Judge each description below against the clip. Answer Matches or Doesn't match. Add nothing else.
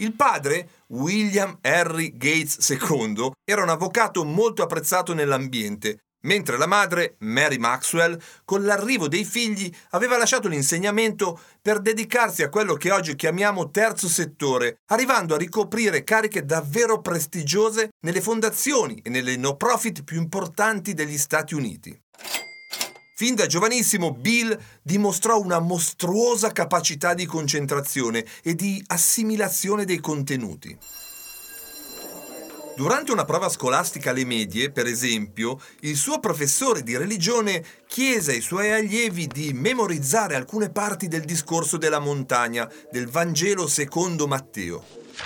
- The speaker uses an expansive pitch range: Matches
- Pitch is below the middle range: Doesn't match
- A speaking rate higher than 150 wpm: Doesn't match